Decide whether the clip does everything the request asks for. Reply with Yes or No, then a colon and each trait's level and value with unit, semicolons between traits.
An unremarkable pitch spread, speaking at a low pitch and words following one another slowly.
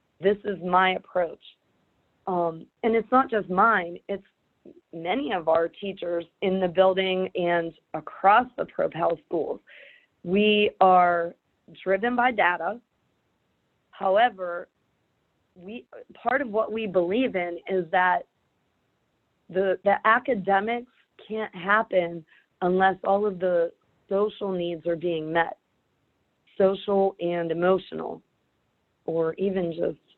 No: average, 3.2 semitones; high, 190 Hz; slow, 115 wpm